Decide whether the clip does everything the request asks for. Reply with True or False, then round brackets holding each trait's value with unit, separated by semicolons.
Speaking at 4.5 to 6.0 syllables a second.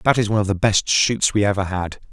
False (6.3 syllables/s)